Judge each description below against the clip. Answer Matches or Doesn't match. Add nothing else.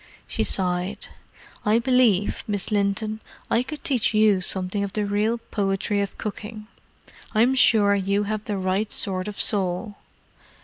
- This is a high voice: Matches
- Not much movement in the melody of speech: Matches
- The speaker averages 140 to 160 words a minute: Matches